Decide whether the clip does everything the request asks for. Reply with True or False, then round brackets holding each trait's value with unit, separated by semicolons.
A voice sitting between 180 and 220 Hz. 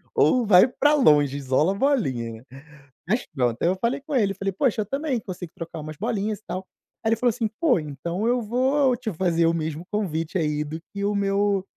True (195 Hz)